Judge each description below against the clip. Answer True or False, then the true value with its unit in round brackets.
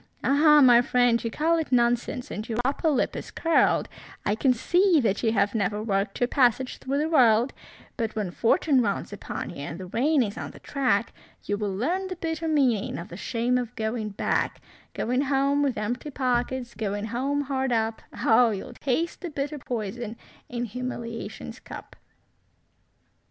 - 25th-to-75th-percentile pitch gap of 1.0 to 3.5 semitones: False (4.2 semitones)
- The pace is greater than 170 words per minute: True (180 wpm)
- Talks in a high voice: True (245 Hz)